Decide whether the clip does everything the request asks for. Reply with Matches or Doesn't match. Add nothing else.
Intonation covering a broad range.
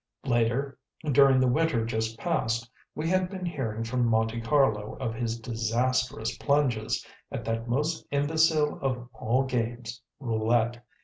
Doesn't match